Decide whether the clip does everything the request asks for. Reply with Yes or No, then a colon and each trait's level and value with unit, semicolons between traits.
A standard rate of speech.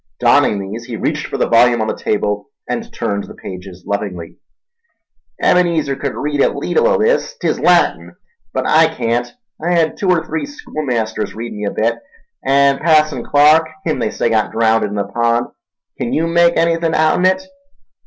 Yes: average, 170 wpm